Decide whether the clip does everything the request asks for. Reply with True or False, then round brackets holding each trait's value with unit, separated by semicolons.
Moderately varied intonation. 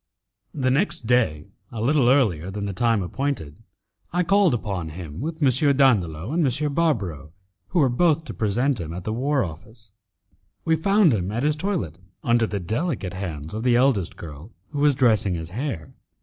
False (7.9 semitones)